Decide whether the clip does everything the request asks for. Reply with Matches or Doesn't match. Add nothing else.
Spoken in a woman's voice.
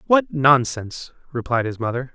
Doesn't match